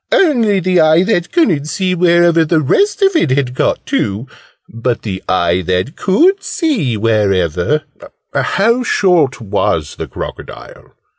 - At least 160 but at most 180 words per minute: No, average, 145 wpm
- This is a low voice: No, medium, 160 Hz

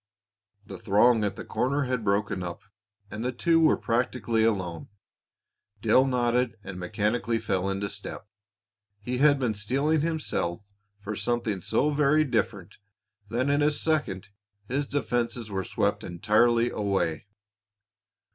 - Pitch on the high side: No, low, 115 Hz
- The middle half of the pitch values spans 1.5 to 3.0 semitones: No, average, 4.5 semitones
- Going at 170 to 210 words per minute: No, slow, 135 wpm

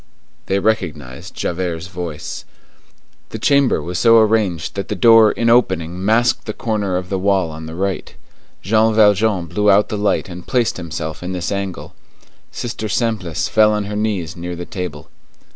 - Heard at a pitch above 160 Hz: No, very low, 95 Hz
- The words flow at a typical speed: Yes, average, 170 wpm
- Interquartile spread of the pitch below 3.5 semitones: No, average, 3.9 semitones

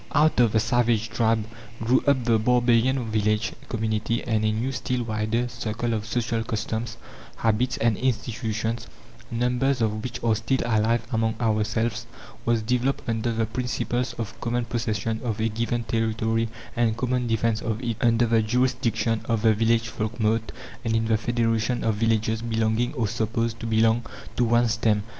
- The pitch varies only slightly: Yes, narrow, 1.4 semitones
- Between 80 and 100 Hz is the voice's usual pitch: No, low, 115 Hz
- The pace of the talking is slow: No, average, 165 wpm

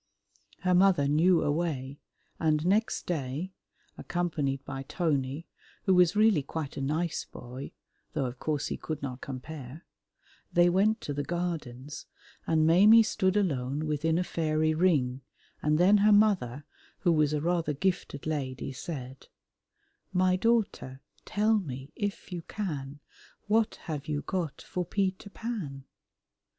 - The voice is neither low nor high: Yes, medium, 160 Hz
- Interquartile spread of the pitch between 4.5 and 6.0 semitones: Yes, average, 4.9 semitones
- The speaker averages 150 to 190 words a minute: No, average, 140 wpm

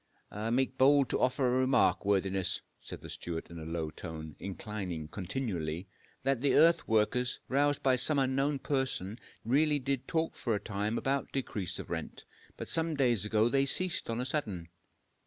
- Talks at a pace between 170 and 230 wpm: Yes, average, 175 wpm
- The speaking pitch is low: Yes, low, 125 Hz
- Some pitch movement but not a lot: No, wide, 5.7 semitones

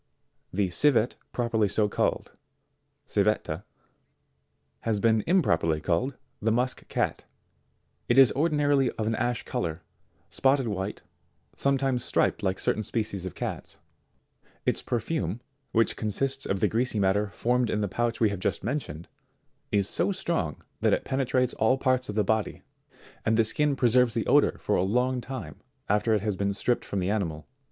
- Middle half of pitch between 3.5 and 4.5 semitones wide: Yes, average, 4.2 semitones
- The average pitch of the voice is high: No, low, 110 Hz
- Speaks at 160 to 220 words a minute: Yes, average, 165 wpm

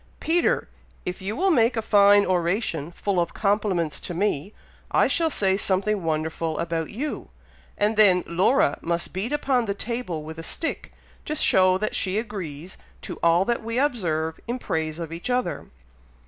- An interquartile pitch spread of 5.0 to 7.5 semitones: Yes, average, 5.3 semitones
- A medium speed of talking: Yes, average, 170 wpm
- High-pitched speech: Yes, high, 195 Hz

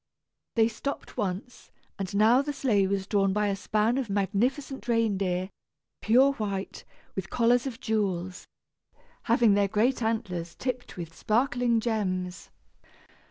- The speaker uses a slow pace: Yes, slow, 130 wpm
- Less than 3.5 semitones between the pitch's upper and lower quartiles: No, average, 3.8 semitones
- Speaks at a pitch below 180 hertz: No, high, 215 Hz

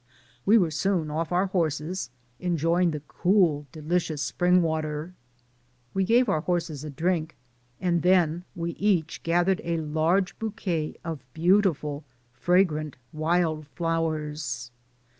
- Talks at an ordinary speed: No, slow, 120 wpm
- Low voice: No, medium, 165 Hz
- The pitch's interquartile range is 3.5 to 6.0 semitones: No, average, 2.7 semitones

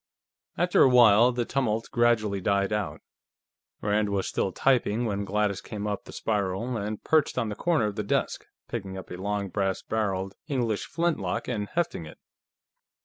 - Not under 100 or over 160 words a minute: No, average, 170 wpm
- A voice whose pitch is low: Yes, low, 105 Hz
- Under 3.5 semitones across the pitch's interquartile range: Yes, average, 3.1 semitones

